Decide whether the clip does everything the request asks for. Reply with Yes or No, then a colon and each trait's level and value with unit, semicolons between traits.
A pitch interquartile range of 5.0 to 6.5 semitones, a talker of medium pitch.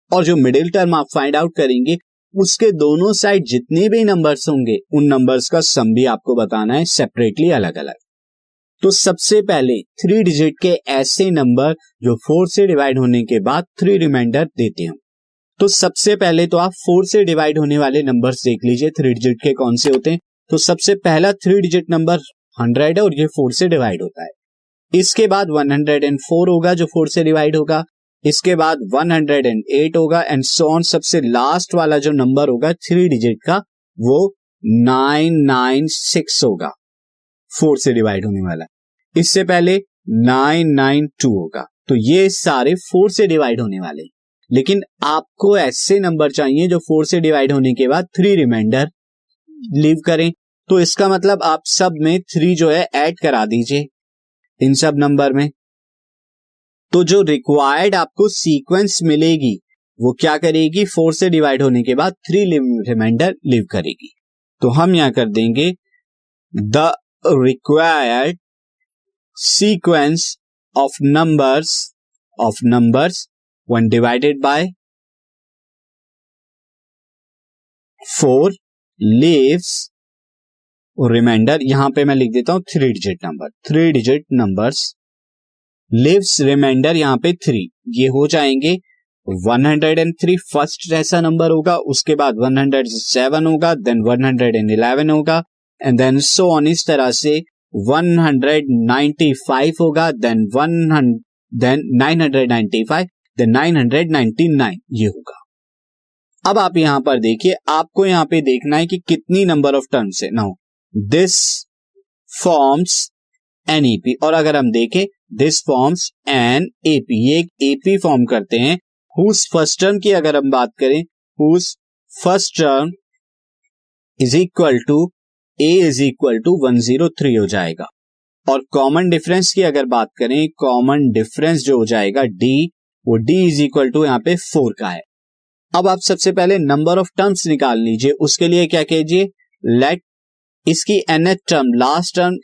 Yes: average, 5.3 semitones; medium, 155 Hz